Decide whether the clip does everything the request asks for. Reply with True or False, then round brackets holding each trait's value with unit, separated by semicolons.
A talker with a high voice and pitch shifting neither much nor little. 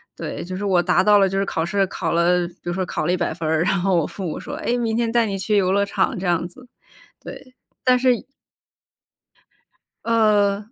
True (195 Hz; 3.9 semitones)